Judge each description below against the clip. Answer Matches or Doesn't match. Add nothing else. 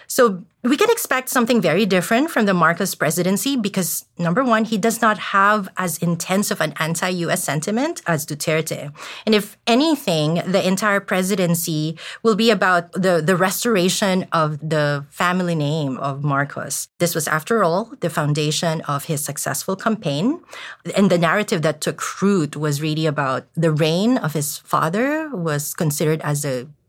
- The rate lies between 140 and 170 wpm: Matches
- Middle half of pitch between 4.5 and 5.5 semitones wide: Matches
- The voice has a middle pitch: Matches